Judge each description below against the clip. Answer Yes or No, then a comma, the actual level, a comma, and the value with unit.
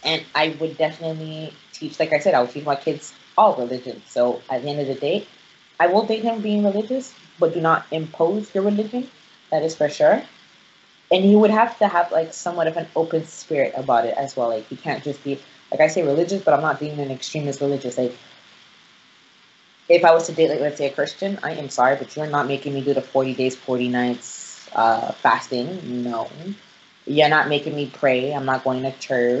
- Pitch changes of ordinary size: Yes, average, 3.8 semitones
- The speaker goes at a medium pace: No, fast, 220 wpm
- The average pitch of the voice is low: No, medium, 150 Hz